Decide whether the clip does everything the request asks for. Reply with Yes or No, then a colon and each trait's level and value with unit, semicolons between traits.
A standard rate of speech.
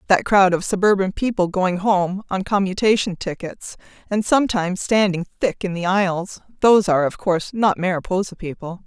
Yes: average, 165 wpm